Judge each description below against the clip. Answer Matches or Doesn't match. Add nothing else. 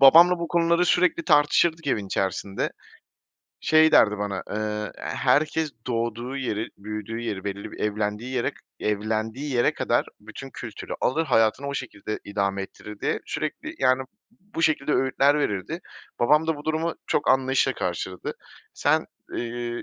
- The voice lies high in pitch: Doesn't match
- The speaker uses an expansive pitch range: Matches